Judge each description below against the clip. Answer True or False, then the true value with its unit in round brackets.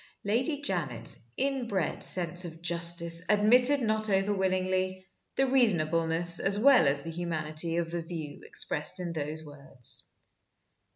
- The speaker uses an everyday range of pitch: True (4.2 semitones)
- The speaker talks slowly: True (130 wpm)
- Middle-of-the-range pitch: True (175 Hz)